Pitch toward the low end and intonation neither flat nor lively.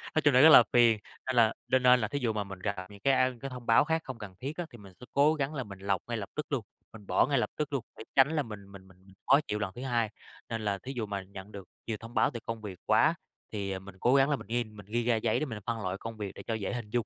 Yes: low, 115 Hz; average, 4.2 semitones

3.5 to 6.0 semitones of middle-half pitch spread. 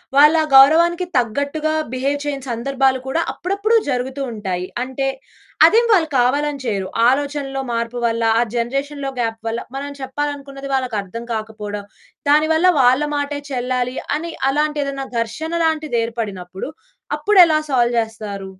Yes: average, 4.1 semitones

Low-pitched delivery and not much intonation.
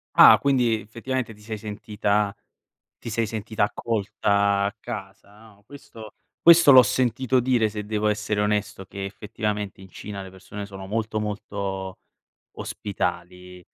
Yes: low, 105 Hz; narrow, 2.1 semitones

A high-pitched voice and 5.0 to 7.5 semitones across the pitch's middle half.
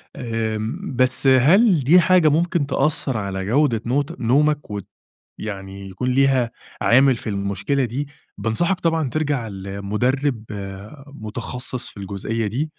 No: low, 125 Hz; average, 5.3 semitones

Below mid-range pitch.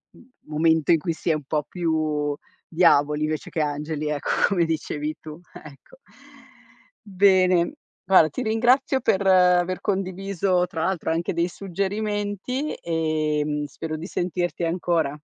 No: medium, 170 Hz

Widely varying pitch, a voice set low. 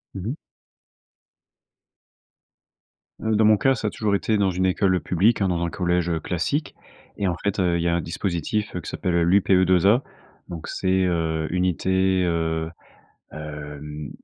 No: average, 2.9 semitones; very low, 90 Hz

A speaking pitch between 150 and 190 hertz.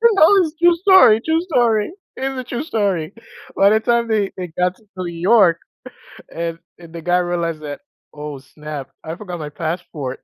Yes: medium, 185 Hz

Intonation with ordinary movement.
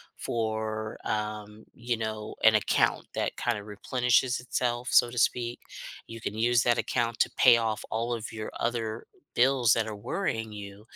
No: narrow, 1.9 semitones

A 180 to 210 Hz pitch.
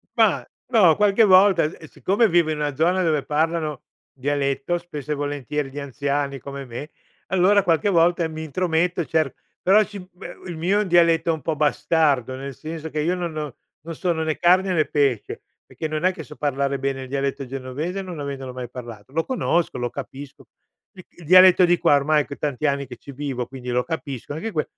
No: medium, 155 Hz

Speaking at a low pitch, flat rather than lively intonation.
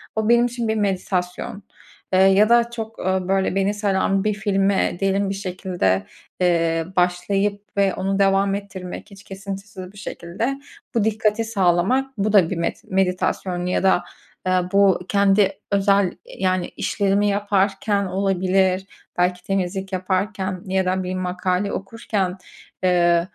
No: high, 195 Hz; narrow, 1.7 semitones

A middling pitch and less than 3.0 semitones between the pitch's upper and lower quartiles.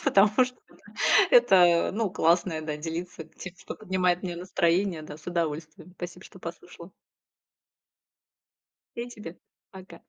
Yes: medium, 175 Hz; narrow, 2.5 semitones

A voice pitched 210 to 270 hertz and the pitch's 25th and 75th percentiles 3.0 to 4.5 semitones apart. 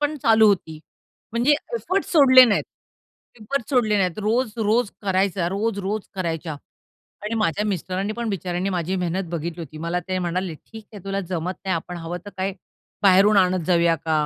No: high, 190 Hz; average, 3.5 semitones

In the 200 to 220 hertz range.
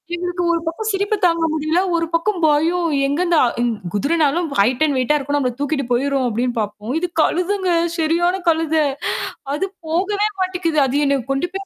No: very high, 325 Hz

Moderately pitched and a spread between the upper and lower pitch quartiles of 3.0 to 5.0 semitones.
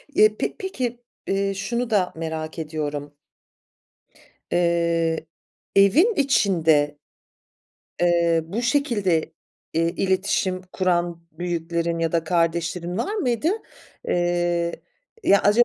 Yes: medium, 175 Hz; average, 3.5 semitones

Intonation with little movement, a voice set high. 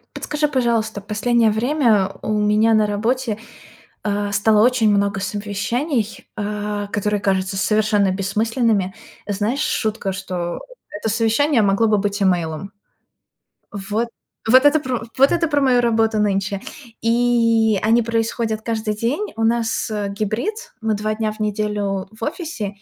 Yes: narrow, 2.3 semitones; high, 215 Hz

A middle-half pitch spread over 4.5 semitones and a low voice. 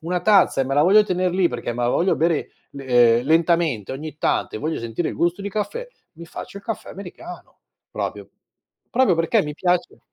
No: wide, 5.4 semitones; medium, 170 Hz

